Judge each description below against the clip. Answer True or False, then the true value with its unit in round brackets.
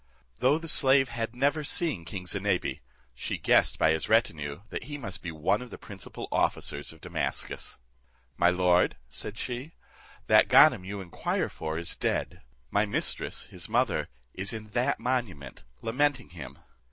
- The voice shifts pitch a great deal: True (6.6 semitones)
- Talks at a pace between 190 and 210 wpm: False (160 wpm)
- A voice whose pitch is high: False (105 Hz)